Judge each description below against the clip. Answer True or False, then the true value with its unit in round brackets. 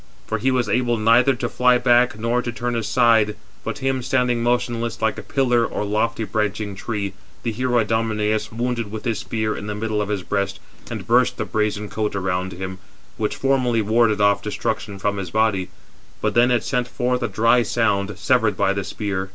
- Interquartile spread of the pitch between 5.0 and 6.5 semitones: False (2.7 semitones)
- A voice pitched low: True (110 Hz)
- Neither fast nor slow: True (195 wpm)